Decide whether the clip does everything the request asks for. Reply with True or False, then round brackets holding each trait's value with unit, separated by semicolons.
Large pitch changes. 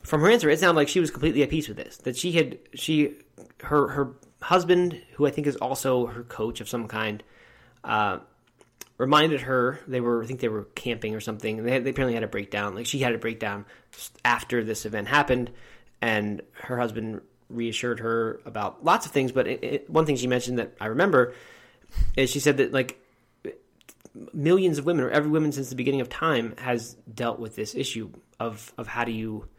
False (4.1 semitones)